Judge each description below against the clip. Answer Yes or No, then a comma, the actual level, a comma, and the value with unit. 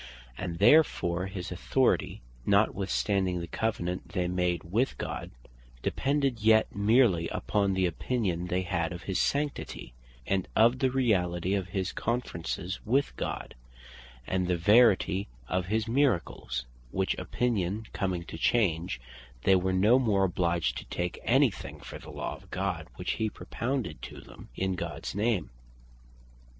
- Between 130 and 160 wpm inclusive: Yes, average, 145 wpm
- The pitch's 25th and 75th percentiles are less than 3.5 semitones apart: No, average, 4.1 semitones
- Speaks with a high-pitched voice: No, very low, 95 Hz